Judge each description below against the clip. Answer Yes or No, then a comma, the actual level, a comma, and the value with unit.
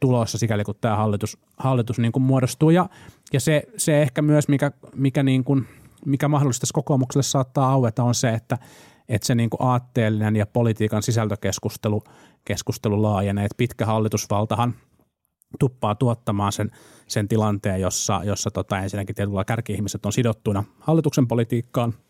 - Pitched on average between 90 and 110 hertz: No, low, 120 Hz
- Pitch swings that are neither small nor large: Yes, average, 4.1 semitones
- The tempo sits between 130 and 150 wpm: Yes, average, 145 wpm